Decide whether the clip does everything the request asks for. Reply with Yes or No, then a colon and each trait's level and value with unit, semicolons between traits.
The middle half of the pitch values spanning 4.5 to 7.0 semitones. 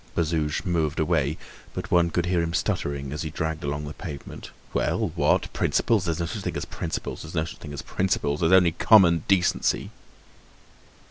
No: narrow, 2.5 semitones